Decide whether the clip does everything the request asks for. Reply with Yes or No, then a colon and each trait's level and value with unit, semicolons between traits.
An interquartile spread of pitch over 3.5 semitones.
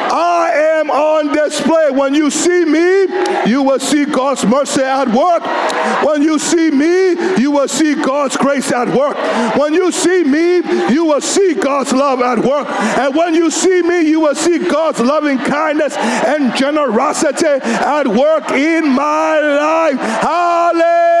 No: average, 3.1 semitones